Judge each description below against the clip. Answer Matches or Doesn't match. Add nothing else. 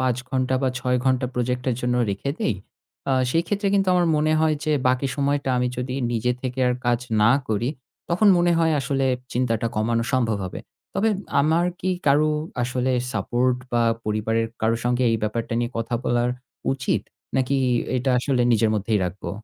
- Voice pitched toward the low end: Matches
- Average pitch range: Matches